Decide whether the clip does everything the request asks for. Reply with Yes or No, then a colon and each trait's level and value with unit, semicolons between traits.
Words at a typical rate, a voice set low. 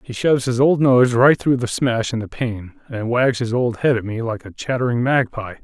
No: fast, 245 wpm; low, 120 Hz